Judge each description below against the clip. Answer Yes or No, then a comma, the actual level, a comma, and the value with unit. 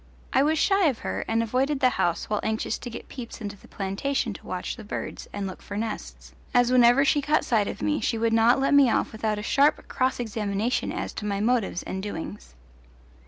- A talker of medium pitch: No, high, 225 Hz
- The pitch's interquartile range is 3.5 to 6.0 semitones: Yes, average, 4.2 semitones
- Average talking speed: No, fast, 220 wpm